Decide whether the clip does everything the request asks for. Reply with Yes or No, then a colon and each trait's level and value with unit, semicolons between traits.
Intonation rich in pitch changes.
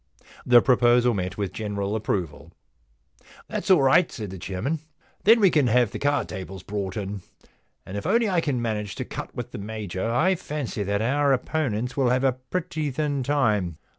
Yes: wide, 5.9 semitones